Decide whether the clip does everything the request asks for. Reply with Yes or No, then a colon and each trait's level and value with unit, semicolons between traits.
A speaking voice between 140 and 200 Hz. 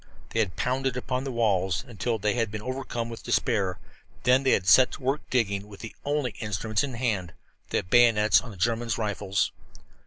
No: low, 115 Hz